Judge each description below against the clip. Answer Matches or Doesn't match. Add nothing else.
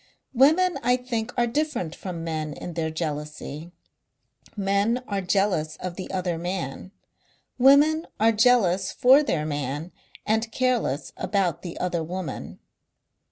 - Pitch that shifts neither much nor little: Doesn't match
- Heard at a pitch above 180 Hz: Matches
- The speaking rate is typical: Doesn't match